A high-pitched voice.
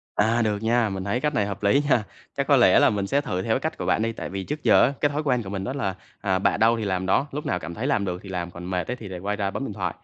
No: low, 105 Hz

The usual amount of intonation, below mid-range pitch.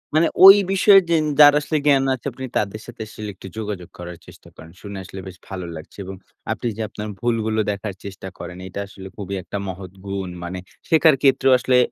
No: wide, 5.7 semitones; low, 105 Hz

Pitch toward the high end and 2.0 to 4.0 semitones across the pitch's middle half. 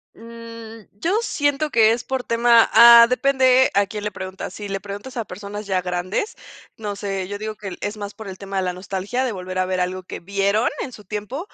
Yes: high, 210 Hz; average, 3.2 semitones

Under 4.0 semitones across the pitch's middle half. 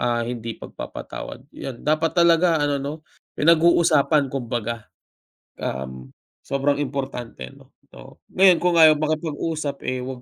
No: average, 4.6 semitones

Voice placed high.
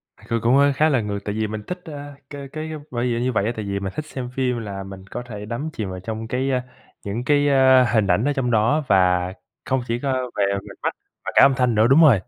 No: low, 120 Hz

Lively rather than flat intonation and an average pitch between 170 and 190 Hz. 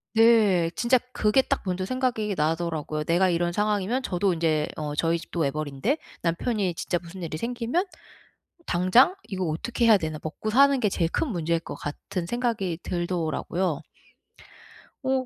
Yes: wide, 5.7 semitones; medium, 185 Hz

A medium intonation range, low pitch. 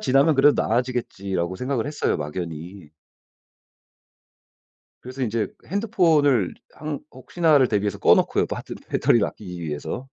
No: wide, 7.3 semitones; low, 125 Hz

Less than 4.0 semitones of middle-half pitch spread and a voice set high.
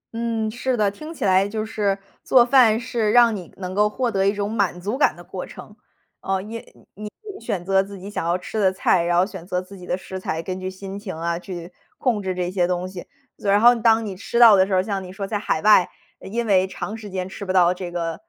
Yes: average, 2.9 semitones; high, 195 Hz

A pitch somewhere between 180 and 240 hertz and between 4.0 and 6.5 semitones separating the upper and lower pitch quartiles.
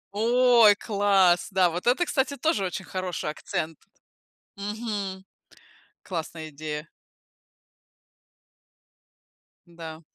Yes: high, 190 Hz; average, 4.8 semitones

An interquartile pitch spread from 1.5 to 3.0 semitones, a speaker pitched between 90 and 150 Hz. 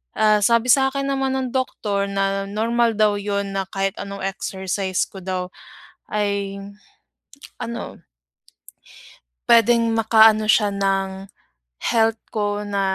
No: narrow, 2.5 semitones; high, 205 Hz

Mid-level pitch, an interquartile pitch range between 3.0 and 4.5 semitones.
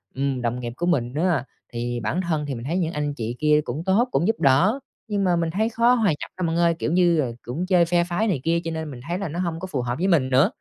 No: medium, 165 Hz; average, 5.1 semitones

